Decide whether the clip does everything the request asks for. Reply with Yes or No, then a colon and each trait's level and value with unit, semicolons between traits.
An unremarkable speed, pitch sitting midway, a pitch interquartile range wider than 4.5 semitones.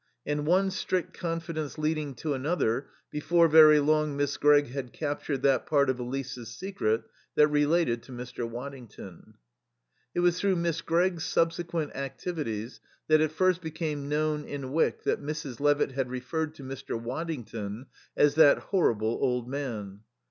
No: average, 150 wpm; medium, 145 Hz; average, 4.0 semitones